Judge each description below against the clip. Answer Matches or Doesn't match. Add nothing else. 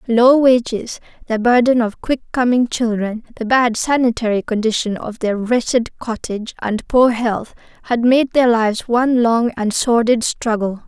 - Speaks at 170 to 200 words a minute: Doesn't match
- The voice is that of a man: Doesn't match